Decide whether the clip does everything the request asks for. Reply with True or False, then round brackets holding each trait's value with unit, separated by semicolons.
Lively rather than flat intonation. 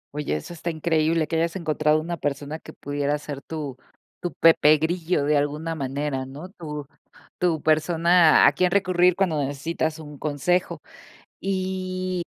False (2.9 semitones)